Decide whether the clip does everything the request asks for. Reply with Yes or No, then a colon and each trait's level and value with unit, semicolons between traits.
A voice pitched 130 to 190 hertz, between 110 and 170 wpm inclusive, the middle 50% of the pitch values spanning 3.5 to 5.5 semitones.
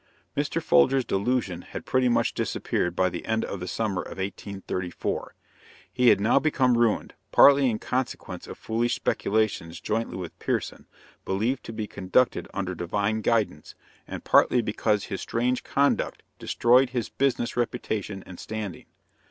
No: low, 110 Hz; average, 150 wpm; average, 4.2 semitones